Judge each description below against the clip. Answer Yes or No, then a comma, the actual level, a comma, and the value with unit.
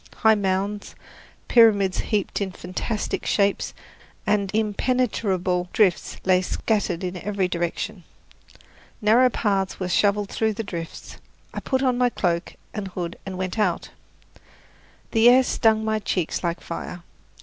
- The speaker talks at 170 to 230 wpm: No, slow, 135 wpm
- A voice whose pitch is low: No, high, 200 Hz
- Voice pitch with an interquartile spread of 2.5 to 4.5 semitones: Yes, average, 3.2 semitones